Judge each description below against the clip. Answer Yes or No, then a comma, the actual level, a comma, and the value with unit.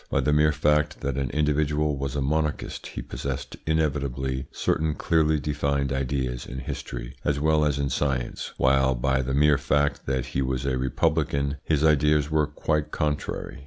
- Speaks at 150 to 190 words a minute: Yes, average, 170 wpm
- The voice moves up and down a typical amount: No, narrow, 2.1 semitones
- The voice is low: Yes, very low, 70 Hz